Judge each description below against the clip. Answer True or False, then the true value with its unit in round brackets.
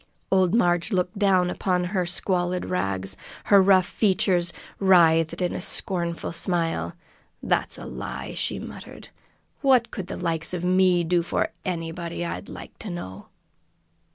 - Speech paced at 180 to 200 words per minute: False (145 wpm)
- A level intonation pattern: True (1.9 semitones)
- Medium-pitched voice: True (180 Hz)